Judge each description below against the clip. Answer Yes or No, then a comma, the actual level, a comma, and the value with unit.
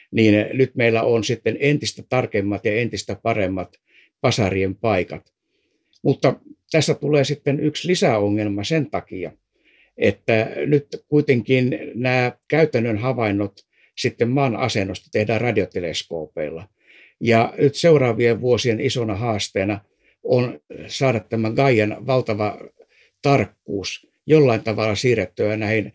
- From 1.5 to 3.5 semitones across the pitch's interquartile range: No, average, 4.4 semitones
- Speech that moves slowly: No, average, 110 wpm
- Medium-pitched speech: No, low, 120 Hz